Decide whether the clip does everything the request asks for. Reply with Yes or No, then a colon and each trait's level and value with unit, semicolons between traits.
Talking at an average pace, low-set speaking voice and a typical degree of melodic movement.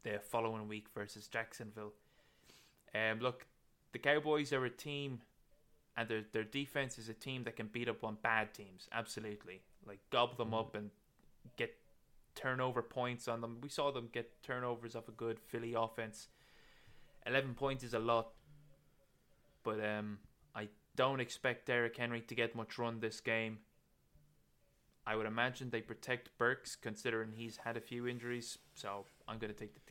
No: average, 165 wpm; low, 115 Hz; narrow, 2.0 semitones